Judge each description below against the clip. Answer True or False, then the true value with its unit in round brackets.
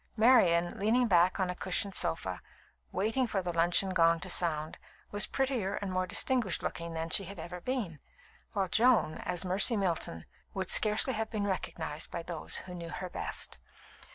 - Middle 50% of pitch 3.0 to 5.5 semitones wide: True (3.9 semitones)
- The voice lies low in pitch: False (185 Hz)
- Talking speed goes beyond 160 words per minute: True (175 wpm)